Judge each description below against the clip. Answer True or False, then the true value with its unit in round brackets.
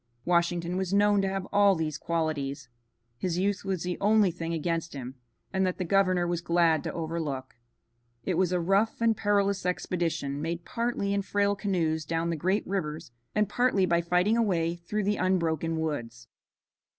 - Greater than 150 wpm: True (175 wpm)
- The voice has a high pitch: False (175 Hz)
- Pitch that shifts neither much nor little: True (3.2 semitones)